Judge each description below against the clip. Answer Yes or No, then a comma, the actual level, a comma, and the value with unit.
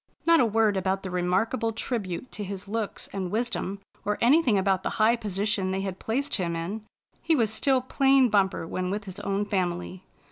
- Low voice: No, high, 205 Hz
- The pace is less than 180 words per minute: No, average, 190 wpm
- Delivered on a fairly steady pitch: No, average, 3.3 semitones